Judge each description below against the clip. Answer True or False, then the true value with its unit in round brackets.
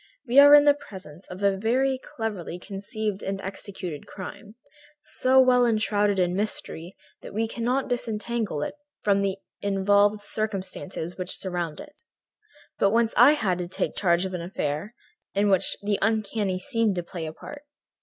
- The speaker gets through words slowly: False (165 wpm)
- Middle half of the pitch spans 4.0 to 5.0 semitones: False (3.5 semitones)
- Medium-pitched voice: False (205 Hz)